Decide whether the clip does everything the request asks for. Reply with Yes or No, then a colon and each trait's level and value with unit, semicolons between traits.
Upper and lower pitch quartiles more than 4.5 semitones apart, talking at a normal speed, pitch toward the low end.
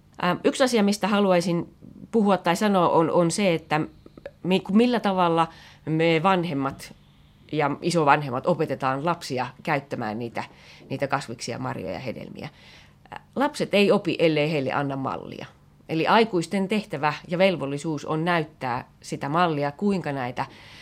No: average, 4.9 semitones; average, 125 wpm; medium, 165 Hz